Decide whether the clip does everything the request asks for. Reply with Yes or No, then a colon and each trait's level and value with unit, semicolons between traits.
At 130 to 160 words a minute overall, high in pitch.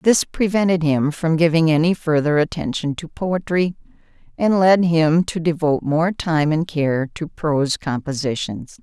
No: average, 150 wpm; medium, 160 Hz